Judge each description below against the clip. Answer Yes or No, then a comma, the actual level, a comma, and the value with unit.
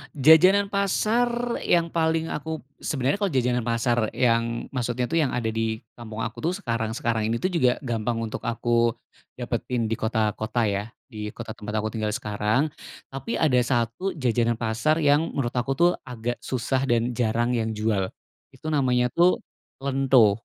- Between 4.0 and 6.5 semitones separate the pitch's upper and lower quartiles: Yes, average, 4.6 semitones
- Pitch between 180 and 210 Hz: No, low, 120 Hz